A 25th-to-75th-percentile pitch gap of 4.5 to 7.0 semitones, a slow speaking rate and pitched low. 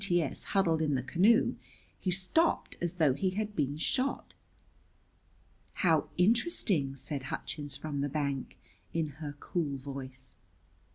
No: average, 4.8 semitones; slow, 130 wpm; medium, 155 Hz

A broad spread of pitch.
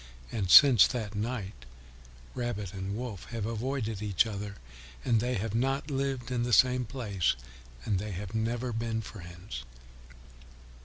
No: average, 3.4 semitones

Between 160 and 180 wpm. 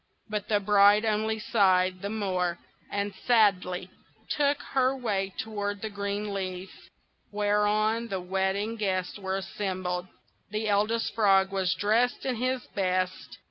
No: slow, 135 wpm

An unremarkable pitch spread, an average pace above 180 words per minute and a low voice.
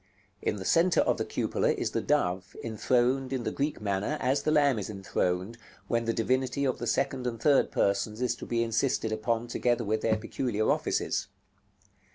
Yes: average, 3.3 semitones; average, 190 wpm; low, 120 Hz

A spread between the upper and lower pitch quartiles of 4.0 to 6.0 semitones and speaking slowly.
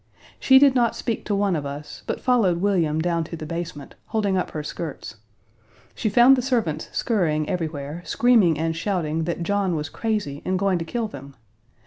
No: wide, 5.5 semitones; average, 185 wpm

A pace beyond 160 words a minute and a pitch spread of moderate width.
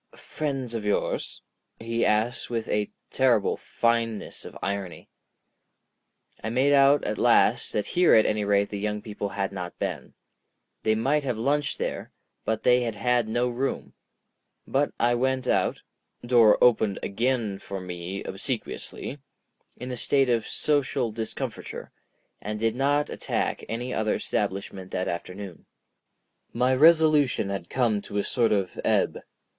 No: average, 140 wpm; average, 3.9 semitones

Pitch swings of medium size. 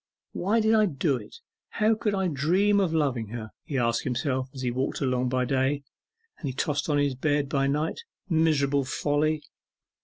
Yes: average, 3.7 semitones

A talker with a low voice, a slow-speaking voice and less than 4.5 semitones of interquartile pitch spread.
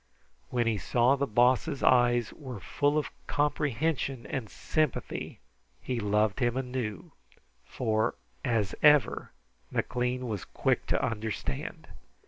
Yes: low, 125 Hz; slow, 115 wpm; average, 3.5 semitones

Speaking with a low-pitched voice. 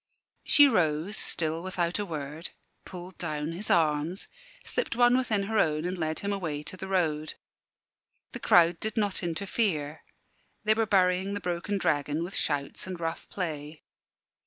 No: medium, 175 Hz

